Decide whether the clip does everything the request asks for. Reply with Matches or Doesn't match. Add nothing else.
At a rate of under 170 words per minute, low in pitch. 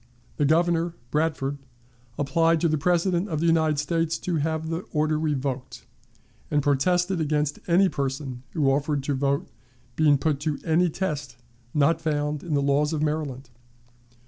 Doesn't match